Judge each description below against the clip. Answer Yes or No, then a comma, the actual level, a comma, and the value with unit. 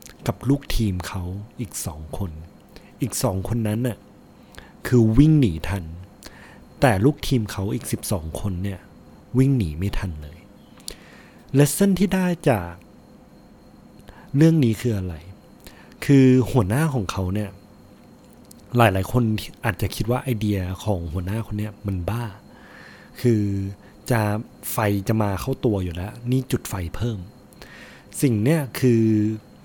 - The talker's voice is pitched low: Yes, low, 105 Hz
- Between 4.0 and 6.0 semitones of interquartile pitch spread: Yes, average, 4.3 semitones